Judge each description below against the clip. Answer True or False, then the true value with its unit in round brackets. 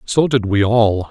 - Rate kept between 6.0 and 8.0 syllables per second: False (4.0 syllables/s)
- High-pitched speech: False (110 Hz)